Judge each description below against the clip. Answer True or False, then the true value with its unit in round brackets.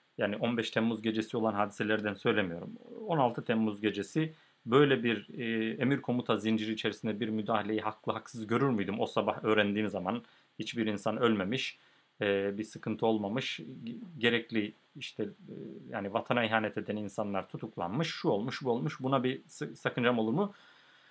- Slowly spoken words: False (140 wpm)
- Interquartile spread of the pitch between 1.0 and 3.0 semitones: True (2.5 semitones)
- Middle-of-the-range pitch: False (110 Hz)